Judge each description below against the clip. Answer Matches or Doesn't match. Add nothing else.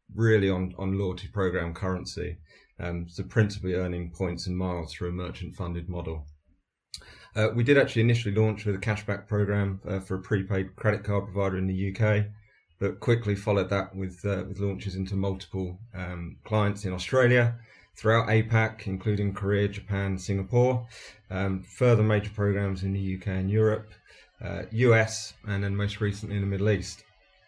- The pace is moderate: Matches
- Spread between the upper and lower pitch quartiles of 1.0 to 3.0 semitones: Matches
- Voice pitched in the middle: Doesn't match